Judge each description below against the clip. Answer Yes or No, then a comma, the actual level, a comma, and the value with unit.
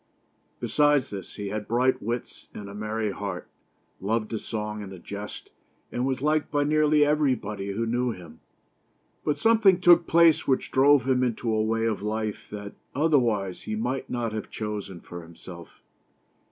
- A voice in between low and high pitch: No, low, 115 Hz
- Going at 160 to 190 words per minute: Yes, average, 165 wpm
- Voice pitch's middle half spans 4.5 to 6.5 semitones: Yes, average, 5.2 semitones